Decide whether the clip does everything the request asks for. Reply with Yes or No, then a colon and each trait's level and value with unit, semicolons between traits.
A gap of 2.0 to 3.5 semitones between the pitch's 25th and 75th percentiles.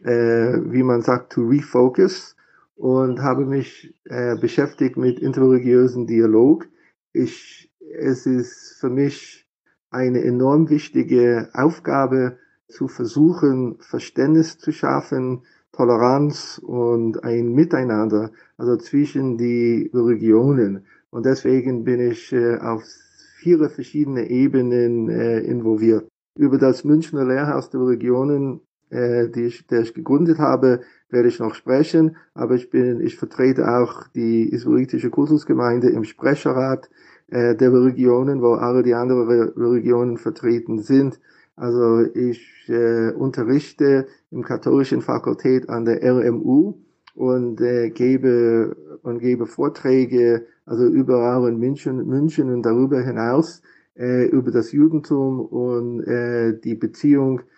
Yes: narrow, 2.4 semitones